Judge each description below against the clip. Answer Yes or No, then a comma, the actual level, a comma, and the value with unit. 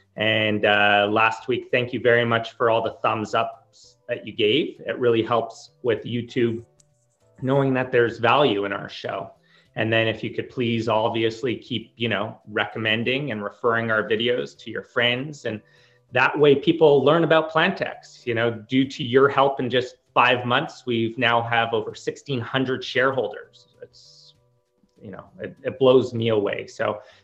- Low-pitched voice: Yes, low, 120 Hz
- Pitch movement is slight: No, average, 3.0 semitones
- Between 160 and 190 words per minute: Yes, average, 170 wpm